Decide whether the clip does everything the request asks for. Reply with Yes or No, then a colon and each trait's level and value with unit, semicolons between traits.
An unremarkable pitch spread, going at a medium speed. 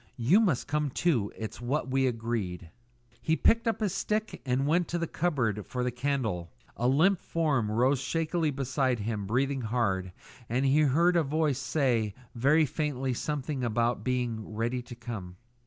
Yes: average, 4.6 semitones; average, 170 wpm